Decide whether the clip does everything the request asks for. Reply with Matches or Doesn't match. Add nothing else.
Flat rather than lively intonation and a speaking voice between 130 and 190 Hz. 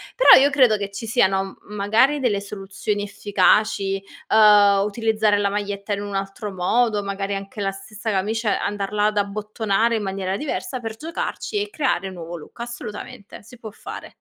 Doesn't match